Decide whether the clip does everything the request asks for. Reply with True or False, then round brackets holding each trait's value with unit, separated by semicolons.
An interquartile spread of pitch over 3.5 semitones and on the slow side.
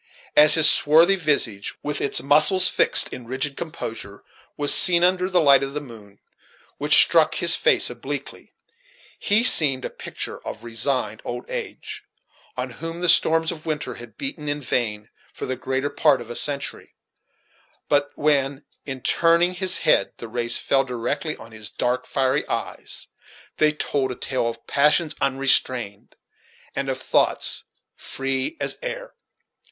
False (4.4 semitones; 155 wpm)